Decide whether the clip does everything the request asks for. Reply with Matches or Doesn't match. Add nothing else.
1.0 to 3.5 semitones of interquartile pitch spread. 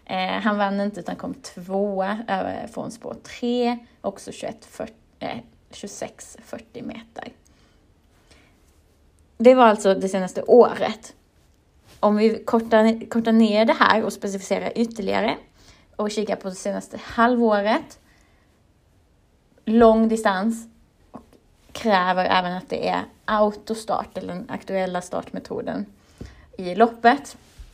Matches